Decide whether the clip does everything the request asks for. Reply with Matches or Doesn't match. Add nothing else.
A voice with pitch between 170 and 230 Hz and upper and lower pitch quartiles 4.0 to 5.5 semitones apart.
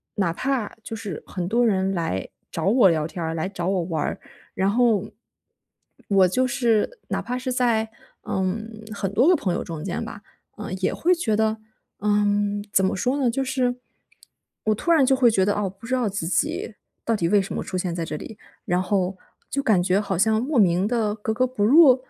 Matches